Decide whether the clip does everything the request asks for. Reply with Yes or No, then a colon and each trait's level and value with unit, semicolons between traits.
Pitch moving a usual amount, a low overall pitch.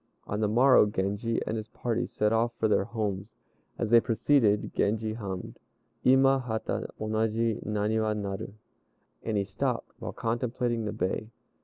No: narrow, 1.8 semitones; low, 110 Hz